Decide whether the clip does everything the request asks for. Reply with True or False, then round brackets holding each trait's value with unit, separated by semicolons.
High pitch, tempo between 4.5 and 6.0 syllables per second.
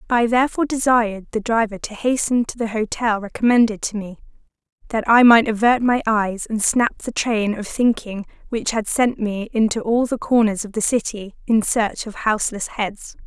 True (225 Hz; 5.0 syllables/s)